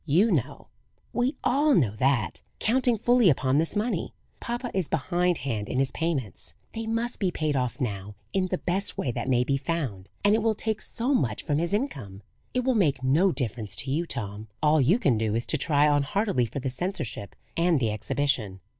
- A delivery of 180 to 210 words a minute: Yes, average, 200 wpm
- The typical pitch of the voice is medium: Yes, medium, 150 Hz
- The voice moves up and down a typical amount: No, wide, 8.3 semitones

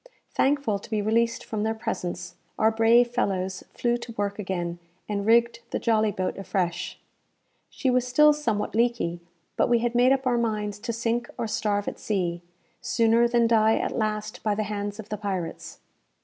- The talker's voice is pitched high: Yes, high, 220 Hz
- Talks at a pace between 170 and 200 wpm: Yes, average, 180 wpm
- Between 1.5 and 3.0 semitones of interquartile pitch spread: Yes, narrow, 2.6 semitones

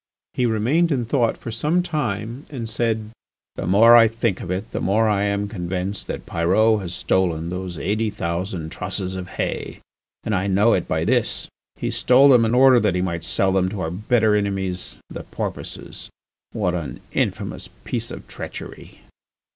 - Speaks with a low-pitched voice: Yes, low, 105 Hz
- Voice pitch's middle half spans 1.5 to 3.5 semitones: No, average, 3.9 semitones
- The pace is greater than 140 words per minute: Yes, average, 180 wpm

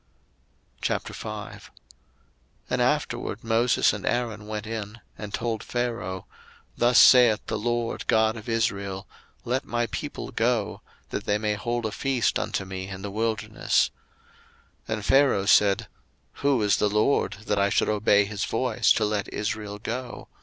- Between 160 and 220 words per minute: No, average, 150 wpm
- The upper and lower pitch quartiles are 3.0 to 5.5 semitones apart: No, narrow, 2.5 semitones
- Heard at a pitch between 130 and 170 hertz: No, low, 110 Hz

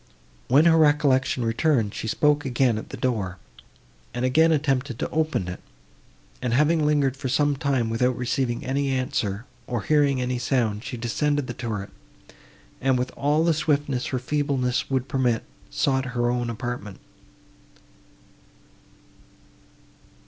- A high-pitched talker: No, low, 130 Hz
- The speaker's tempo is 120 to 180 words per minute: Yes, average, 140 wpm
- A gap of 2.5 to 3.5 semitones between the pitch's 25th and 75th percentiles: Yes, average, 3.2 semitones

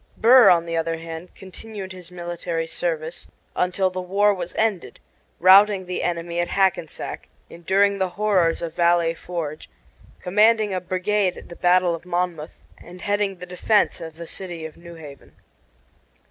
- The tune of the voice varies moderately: No, narrow, 2.3 semitones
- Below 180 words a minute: Yes, average, 160 wpm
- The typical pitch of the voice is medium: Yes, medium, 180 Hz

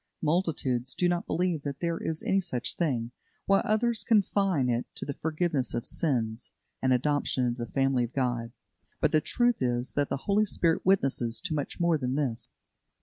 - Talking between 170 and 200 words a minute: Yes, average, 185 wpm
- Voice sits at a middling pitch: Yes, medium, 145 Hz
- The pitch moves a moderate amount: No, wide, 5.9 semitones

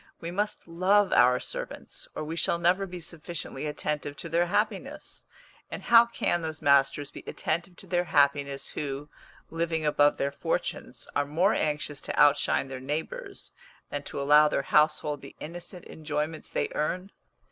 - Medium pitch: Yes, medium, 155 Hz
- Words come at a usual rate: Yes, average, 160 wpm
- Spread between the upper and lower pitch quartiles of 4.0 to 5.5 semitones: No, average, 3.2 semitones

